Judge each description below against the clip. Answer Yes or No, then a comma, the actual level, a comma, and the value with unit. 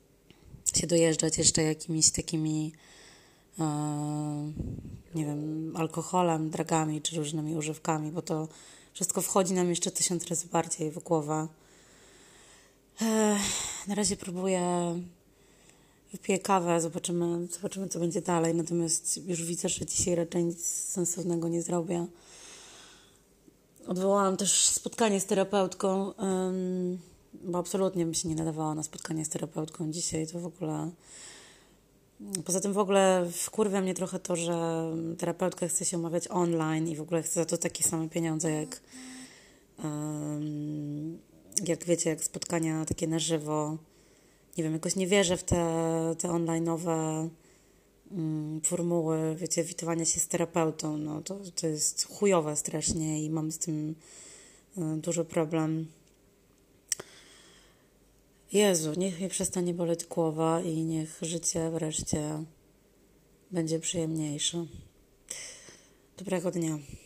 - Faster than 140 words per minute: No, average, 125 wpm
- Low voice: No, medium, 165 Hz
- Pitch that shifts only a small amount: Yes, narrow, 2.2 semitones